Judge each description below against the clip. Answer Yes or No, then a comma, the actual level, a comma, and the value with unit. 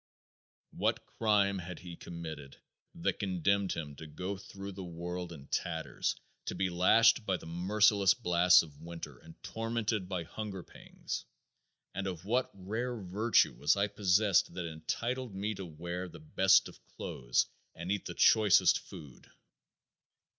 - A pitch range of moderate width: Yes, average, 3.3 semitones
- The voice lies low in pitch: Yes, very low, 95 Hz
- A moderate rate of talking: Yes, average, 150 wpm